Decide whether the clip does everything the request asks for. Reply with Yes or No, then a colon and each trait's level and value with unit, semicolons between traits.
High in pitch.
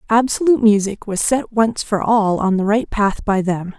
Yes: high, 210 Hz